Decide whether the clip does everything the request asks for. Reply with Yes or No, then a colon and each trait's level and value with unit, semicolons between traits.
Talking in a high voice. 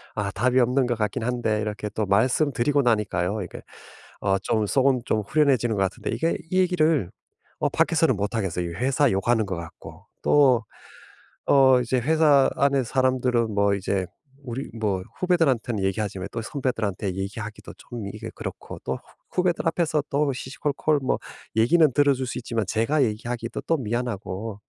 No: low, 120 Hz